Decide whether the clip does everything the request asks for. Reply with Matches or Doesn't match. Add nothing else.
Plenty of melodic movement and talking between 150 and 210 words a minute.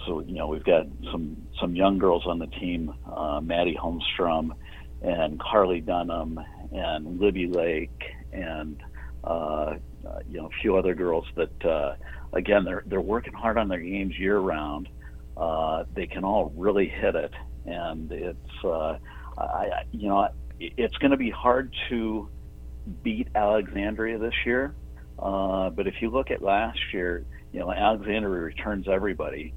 Matches